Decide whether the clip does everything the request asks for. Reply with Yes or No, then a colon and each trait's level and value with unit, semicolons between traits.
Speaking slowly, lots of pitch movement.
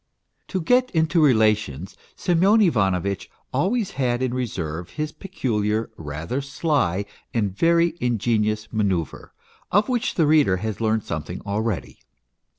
Yes: slow, 125 wpm; wide, 8.2 semitones